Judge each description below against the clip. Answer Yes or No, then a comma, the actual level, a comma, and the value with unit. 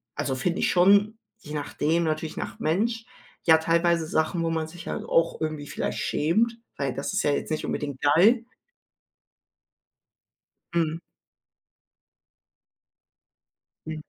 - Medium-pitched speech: Yes, medium, 165 Hz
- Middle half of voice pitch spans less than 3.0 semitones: Yes, narrow, 2.6 semitones